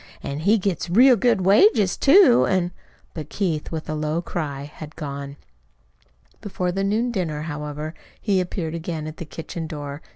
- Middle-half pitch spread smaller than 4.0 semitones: No, average, 4.4 semitones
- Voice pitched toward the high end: No, medium, 170 Hz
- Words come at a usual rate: Yes, average, 170 wpm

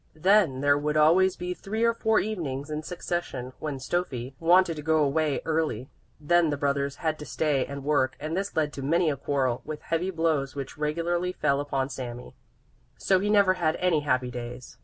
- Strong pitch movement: No, average, 3.9 semitones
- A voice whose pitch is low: No, medium, 155 Hz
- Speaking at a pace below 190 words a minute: No, average, 195 wpm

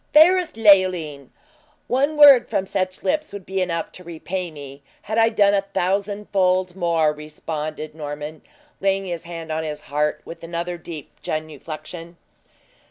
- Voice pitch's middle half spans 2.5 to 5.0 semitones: Yes, average, 4.1 semitones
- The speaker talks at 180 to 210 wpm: No, average, 145 wpm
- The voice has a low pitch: No, medium, 175 Hz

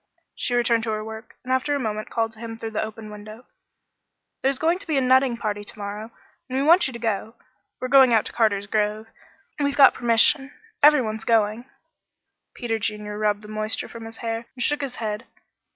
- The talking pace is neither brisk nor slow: No, fast, 210 wpm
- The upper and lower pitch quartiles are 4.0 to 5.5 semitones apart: No, average, 3.2 semitones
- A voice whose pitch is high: Yes, high, 225 Hz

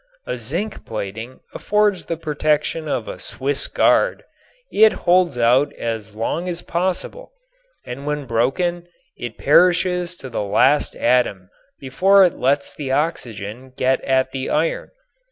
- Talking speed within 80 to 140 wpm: Yes, slow, 135 wpm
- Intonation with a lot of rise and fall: Yes, wide, 5.9 semitones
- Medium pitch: Yes, medium, 145 Hz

